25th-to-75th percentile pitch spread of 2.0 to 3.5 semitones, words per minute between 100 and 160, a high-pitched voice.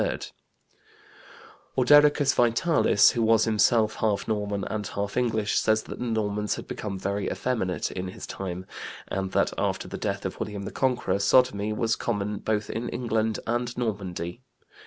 No: average, 2.9 semitones; average, 155 wpm; low, 110 Hz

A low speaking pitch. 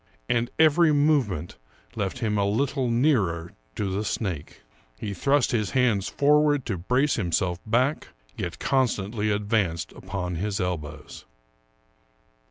Yes: low, 105 Hz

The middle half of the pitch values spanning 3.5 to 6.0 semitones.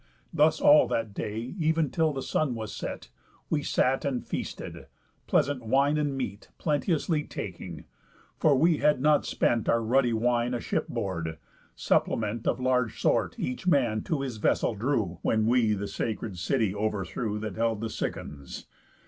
Yes: average, 5.0 semitones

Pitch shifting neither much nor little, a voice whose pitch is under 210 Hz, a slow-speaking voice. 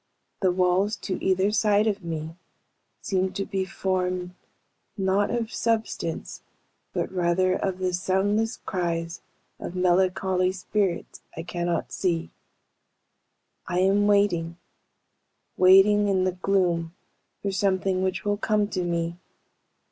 No: narrow, 2.0 semitones; medium, 185 Hz; slow, 125 wpm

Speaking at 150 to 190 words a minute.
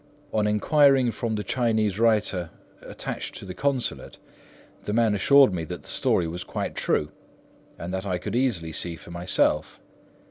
Yes: average, 165 wpm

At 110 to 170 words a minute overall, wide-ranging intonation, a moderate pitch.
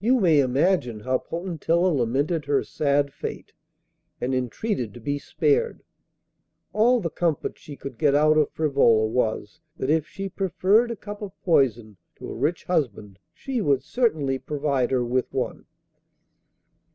Yes: average, 150 wpm; wide, 6.1 semitones; medium, 145 Hz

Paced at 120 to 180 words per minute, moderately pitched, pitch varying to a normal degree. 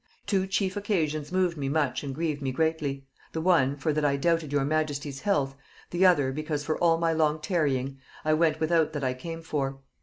No: fast, 205 wpm; medium, 155 Hz; average, 3.0 semitones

